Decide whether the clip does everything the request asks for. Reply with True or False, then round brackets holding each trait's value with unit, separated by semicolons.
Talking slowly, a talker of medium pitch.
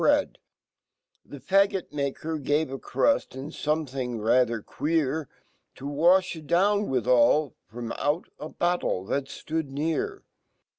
True (90 wpm; 150 Hz)